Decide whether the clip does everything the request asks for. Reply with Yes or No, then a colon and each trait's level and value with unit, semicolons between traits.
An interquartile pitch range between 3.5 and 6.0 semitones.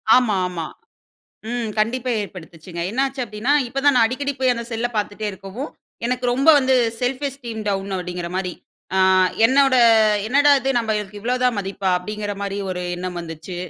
Yes: average, 4.9 semitones